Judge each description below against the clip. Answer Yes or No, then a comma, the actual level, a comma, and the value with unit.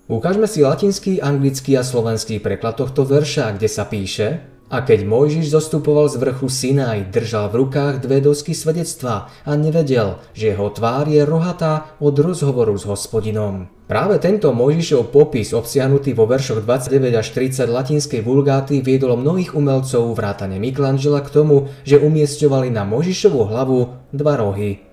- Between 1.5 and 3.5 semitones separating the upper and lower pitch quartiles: No, average, 4.4 semitones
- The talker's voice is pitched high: No, low, 135 Hz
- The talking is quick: No, average, 150 wpm